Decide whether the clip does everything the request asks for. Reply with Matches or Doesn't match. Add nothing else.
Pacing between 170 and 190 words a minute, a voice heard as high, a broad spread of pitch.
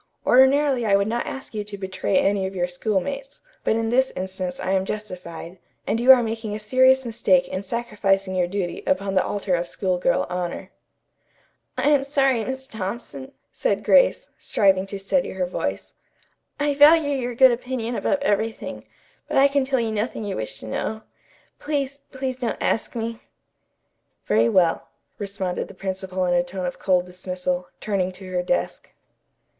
Matches